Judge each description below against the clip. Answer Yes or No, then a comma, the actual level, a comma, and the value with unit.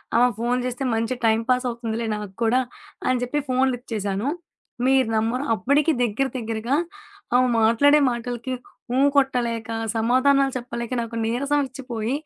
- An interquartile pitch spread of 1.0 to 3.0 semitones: Yes, narrow, 2.5 semitones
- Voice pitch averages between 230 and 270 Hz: Yes, high, 245 Hz